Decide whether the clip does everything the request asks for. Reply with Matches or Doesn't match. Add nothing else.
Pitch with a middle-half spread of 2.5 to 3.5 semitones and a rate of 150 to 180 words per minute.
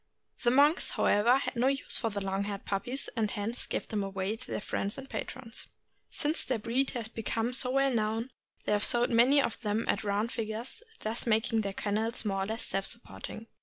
Doesn't match